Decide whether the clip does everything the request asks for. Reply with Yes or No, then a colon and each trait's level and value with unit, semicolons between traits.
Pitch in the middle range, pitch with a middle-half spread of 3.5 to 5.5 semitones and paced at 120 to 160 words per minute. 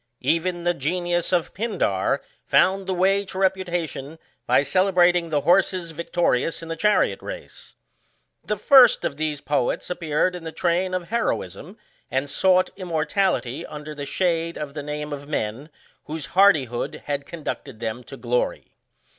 Yes: medium, 170 Hz; average, 4.0 semitones; average, 155 wpm